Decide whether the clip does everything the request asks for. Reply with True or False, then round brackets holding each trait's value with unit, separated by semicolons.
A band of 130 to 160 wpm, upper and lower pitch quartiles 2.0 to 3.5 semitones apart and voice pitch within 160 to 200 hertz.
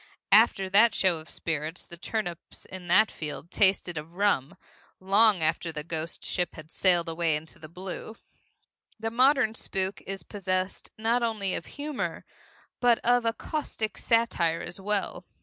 False (155 wpm; 4.9 semitones; 190 Hz)